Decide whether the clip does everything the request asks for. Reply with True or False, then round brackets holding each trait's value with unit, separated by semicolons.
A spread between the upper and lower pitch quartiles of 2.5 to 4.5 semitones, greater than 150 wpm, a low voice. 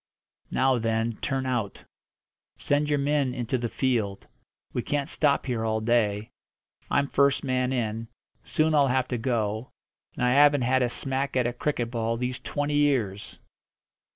True (3.4 semitones; 160 wpm; 125 Hz)